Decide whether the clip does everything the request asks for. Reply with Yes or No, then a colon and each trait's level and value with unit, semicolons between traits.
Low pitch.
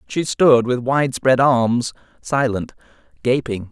Yes: low, 125 Hz